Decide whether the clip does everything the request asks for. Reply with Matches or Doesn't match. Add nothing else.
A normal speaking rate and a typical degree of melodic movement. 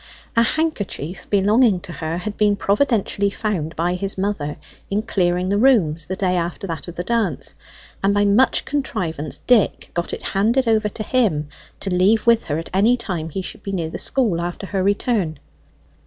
Matches